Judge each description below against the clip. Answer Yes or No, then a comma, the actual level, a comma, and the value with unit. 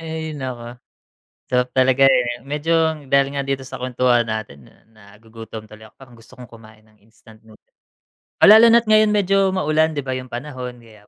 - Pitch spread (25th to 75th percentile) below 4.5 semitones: No, average, 5.1 semitones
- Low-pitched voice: Yes, low, 125 Hz